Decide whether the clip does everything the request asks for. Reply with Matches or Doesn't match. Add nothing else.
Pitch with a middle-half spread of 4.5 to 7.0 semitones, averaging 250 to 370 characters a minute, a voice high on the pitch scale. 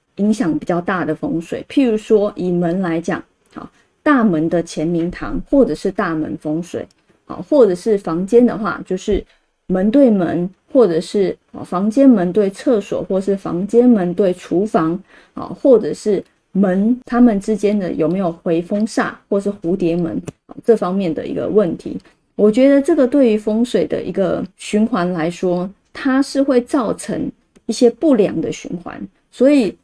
Doesn't match